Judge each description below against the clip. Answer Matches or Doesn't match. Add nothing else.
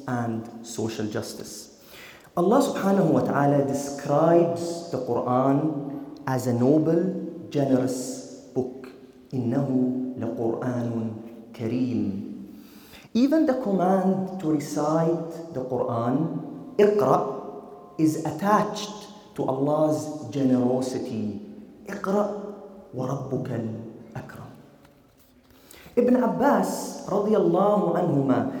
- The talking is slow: Matches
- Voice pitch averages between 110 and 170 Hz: Matches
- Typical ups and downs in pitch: Doesn't match